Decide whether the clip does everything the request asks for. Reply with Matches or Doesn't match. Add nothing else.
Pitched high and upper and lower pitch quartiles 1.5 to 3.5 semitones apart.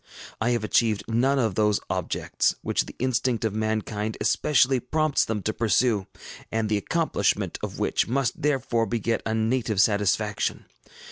Doesn't match